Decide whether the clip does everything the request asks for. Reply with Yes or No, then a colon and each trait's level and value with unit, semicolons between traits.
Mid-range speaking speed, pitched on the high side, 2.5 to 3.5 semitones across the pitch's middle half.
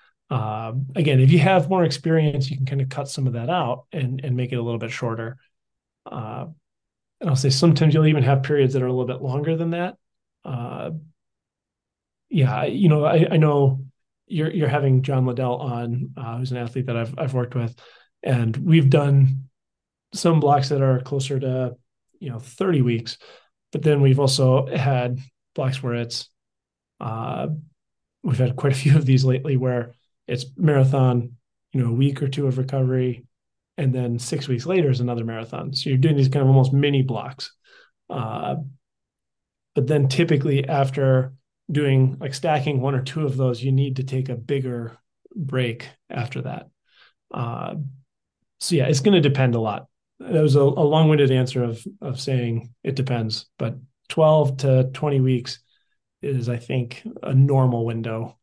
No: average, 180 wpm; low, 135 Hz; average, 2.9 semitones